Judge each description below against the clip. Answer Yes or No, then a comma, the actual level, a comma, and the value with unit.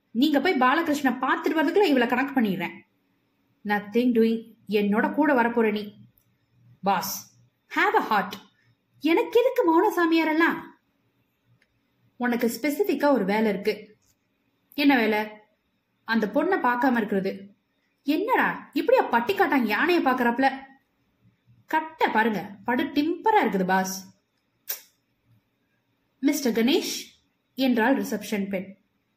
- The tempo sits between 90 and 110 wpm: Yes, average, 105 wpm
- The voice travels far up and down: Yes, wide, 6.5 semitones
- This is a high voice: Yes, very high, 250 Hz